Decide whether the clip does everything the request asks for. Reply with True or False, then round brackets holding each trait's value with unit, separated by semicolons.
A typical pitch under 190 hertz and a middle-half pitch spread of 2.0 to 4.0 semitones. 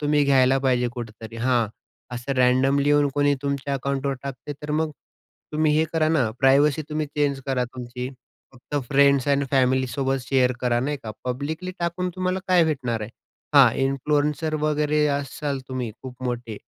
True (140 Hz; 2.8 semitones)